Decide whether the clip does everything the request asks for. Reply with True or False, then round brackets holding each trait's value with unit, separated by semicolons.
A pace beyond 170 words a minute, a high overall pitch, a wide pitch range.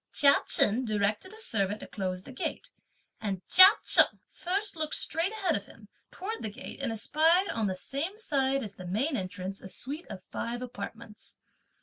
True (185 wpm; 245 Hz; 8.1 semitones)